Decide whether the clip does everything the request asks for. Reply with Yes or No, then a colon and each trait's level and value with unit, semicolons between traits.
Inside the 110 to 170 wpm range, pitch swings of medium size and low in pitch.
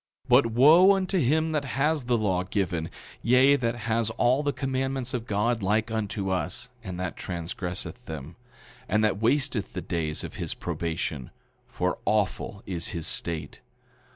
No: average, 160 wpm; wide, 6.4 semitones; low, 110 Hz